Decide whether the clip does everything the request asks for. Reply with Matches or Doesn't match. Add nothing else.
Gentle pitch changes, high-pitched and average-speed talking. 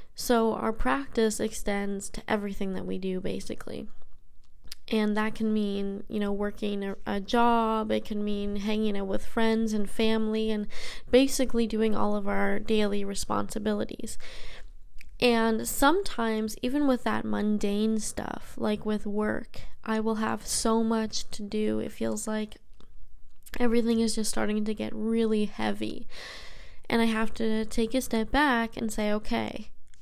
Matches